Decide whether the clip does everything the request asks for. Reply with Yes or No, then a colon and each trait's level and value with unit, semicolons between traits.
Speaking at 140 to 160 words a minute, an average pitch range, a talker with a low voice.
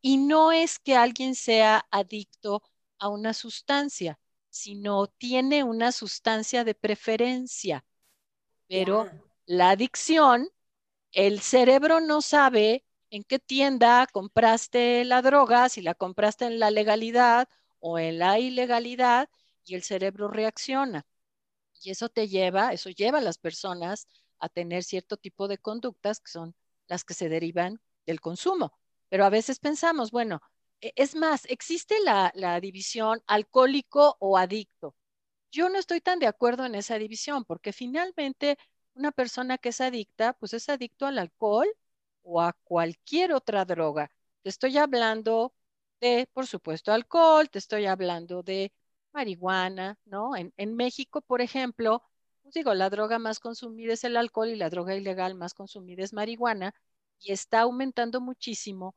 No: average, 150 wpm; average, 4.7 semitones; high, 225 Hz